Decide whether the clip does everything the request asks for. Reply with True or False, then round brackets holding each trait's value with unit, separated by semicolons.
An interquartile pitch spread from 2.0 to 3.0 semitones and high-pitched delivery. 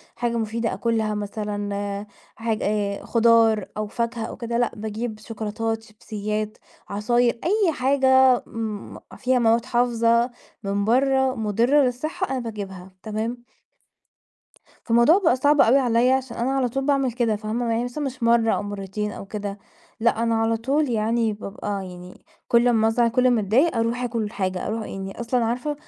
True (2.5 semitones; 230 Hz)